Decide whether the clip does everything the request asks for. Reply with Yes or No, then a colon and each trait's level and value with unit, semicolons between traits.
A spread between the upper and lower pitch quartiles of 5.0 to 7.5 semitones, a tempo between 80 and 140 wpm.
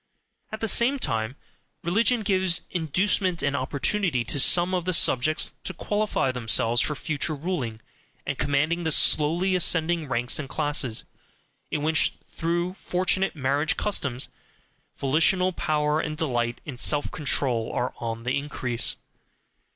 Yes: wide, 5.6 semitones; slow, 135 wpm